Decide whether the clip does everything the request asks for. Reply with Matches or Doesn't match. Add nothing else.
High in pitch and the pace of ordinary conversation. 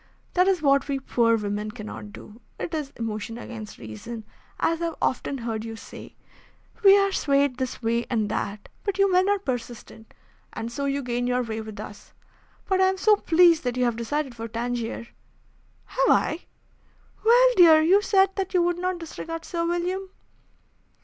Matches